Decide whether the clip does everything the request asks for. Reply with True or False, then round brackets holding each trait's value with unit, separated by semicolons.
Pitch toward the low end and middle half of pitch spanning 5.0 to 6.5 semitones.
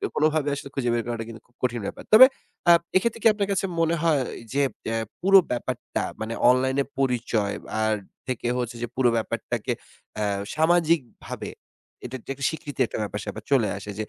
True (130 Hz; 5.4 semitones)